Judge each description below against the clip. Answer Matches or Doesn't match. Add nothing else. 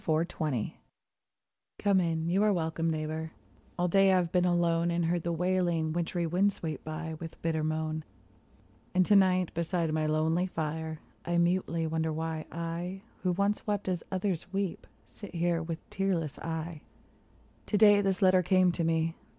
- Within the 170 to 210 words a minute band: Matches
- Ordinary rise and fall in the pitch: Doesn't match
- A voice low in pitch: Doesn't match